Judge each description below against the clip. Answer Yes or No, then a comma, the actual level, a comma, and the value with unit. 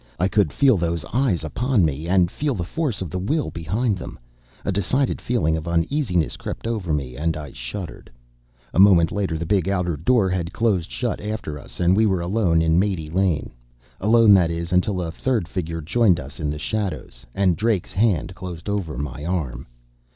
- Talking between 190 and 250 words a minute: Yes, average, 195 wpm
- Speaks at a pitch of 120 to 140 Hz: No, very low, 90 Hz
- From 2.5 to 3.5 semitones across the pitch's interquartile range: No, average, 4.3 semitones